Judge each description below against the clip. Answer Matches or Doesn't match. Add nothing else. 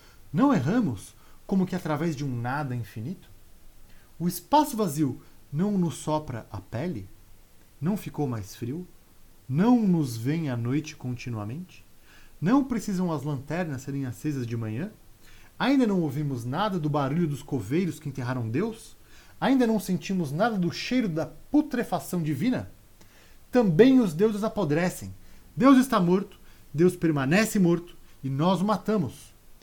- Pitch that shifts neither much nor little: Doesn't match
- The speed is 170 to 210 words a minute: Doesn't match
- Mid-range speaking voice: Matches